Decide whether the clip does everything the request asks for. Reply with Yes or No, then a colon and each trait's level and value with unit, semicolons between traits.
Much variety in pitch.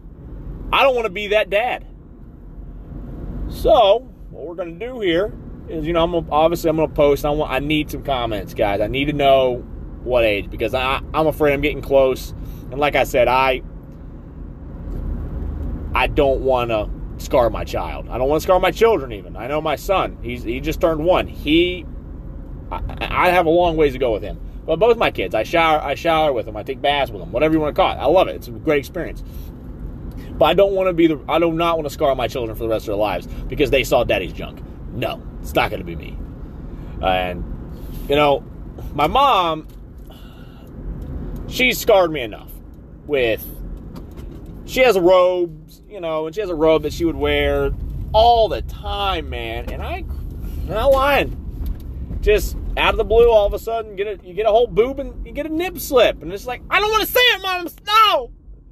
Yes: wide, 9.0 semitones